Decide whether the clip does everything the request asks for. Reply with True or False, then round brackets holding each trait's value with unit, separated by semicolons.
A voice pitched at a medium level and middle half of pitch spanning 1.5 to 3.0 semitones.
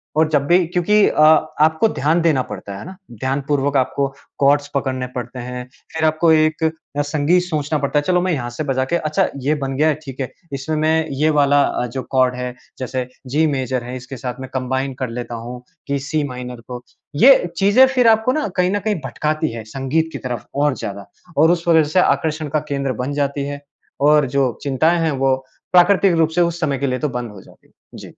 False (145 Hz; 3.7 semitones)